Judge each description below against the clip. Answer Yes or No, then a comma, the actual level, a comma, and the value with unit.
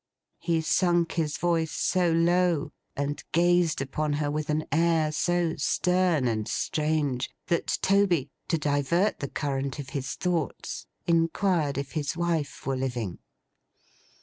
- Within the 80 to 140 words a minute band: Yes, slow, 135 wpm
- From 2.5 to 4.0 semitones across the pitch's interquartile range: Yes, average, 3.3 semitones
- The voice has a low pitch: No, medium, 155 Hz